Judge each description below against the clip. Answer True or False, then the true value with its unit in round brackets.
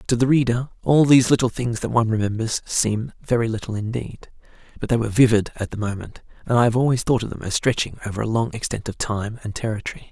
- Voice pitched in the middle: False (115 Hz)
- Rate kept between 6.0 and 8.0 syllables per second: True (6.4 syllables/s)